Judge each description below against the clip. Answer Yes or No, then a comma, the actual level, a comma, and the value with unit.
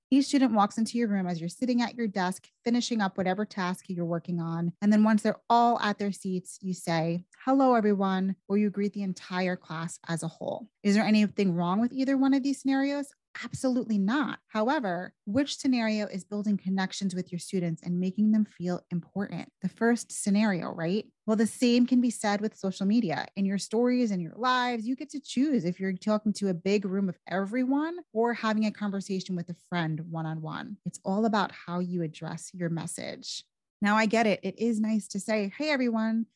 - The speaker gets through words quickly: Yes, fast, 210 wpm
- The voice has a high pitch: Yes, high, 205 Hz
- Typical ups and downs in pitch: Yes, average, 4.3 semitones